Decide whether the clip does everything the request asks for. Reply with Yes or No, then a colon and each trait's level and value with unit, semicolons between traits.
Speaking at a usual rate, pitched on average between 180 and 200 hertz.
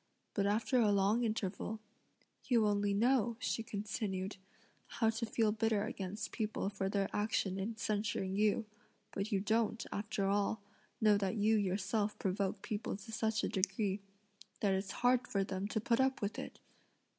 No: average, 165 wpm; high, 210 Hz